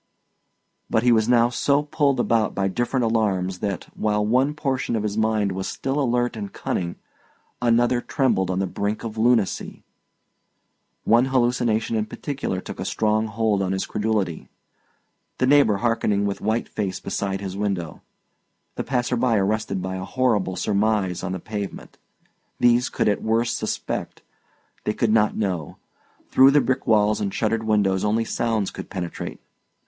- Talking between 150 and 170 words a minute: Yes, average, 160 wpm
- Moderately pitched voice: No, low, 110 Hz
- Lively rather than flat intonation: No, average, 3.4 semitones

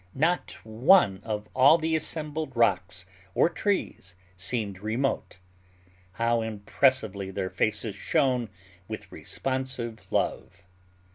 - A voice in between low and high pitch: No, low, 115 Hz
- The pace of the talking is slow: Yes, slow, 100 wpm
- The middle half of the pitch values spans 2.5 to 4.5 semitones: No, average, 5.1 semitones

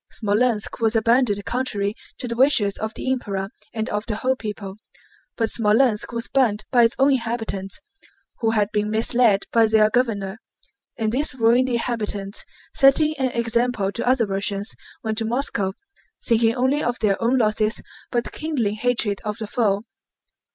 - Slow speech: No, average, 160 wpm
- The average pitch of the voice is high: Yes, high, 225 Hz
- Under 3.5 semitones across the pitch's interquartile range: Yes, average, 2.9 semitones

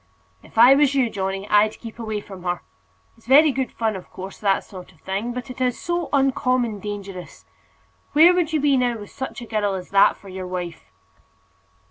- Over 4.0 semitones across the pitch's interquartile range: Yes, average, 5.2 semitones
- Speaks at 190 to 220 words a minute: Yes, average, 200 wpm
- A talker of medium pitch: No, high, 220 Hz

